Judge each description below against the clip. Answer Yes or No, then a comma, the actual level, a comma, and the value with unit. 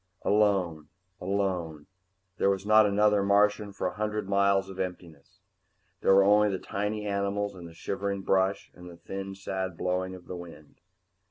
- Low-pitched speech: Yes, very low, 95 Hz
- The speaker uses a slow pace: No, average, 165 wpm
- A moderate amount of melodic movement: No, narrow, 2.0 semitones